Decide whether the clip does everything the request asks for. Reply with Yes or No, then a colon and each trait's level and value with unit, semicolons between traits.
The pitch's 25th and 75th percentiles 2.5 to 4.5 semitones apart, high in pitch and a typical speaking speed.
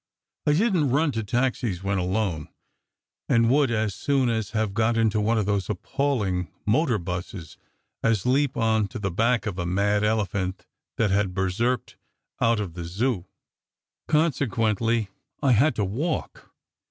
No: average, 4.2 semitones; low, 110 Hz; average, 155 wpm